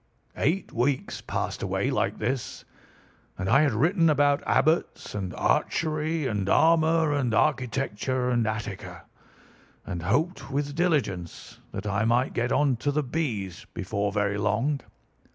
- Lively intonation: Yes, wide, 6.3 semitones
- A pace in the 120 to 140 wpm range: Yes, slow, 135 wpm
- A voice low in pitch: Yes, low, 130 Hz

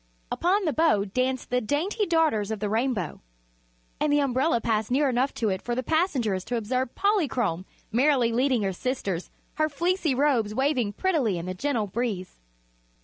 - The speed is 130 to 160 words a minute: No, average, 170 wpm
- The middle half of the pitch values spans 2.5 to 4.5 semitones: No, wide, 5.5 semitones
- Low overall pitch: No, very high, 250 Hz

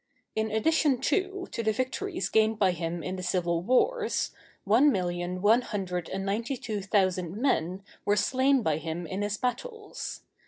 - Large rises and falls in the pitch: Yes, wide, 6.0 semitones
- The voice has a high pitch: Yes, high, 210 Hz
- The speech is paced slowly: No, average, 165 wpm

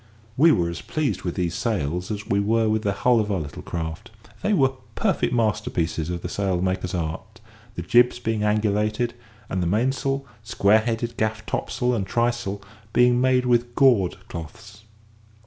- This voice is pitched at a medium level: No, low, 110 Hz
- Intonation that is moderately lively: Yes, average, 4.6 semitones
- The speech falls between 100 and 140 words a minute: No, average, 165 wpm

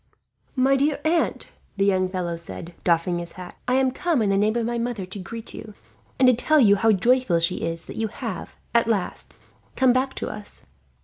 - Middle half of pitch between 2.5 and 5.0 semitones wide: No, wide, 5.5 semitones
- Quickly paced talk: Yes, fast, 210 wpm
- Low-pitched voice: No, high, 220 Hz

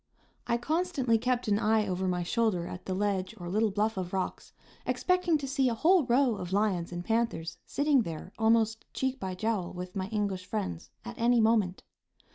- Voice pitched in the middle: No, high, 215 Hz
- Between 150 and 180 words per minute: No, average, 190 wpm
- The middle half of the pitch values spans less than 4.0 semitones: No, average, 4.5 semitones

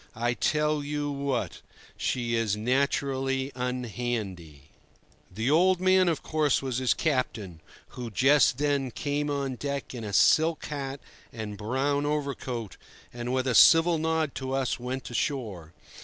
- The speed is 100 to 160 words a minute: Yes, average, 140 wpm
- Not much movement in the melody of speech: No, average, 3.5 semitones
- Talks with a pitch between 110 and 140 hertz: Yes, low, 135 Hz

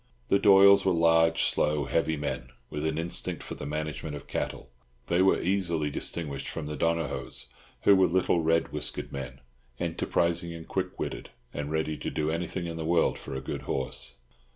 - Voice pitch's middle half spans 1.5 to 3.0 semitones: Yes, narrow, 2.4 semitones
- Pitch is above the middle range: No, very low, 80 Hz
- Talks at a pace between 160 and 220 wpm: Yes, average, 180 wpm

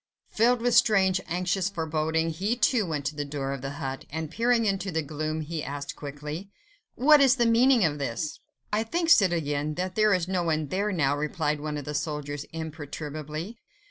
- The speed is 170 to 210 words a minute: Yes, average, 190 wpm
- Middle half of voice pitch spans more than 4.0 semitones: Yes, wide, 5.4 semitones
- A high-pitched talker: No, medium, 160 Hz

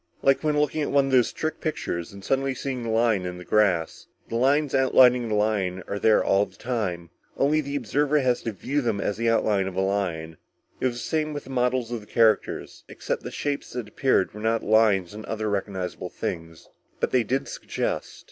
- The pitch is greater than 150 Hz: No, low, 115 Hz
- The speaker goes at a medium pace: No, fast, 220 wpm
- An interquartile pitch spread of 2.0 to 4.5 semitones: No, average, 5.0 semitones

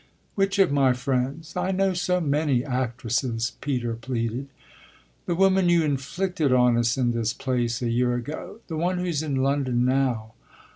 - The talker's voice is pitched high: No, low, 135 Hz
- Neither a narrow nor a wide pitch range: Yes, average, 5.0 semitones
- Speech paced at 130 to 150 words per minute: No, average, 160 wpm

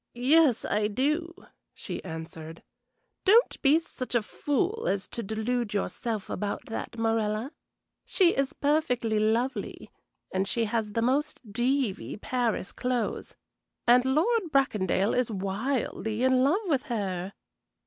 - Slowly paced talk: Yes, slow, 130 wpm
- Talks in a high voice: Yes, high, 240 Hz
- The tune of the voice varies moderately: Yes, average, 4.5 semitones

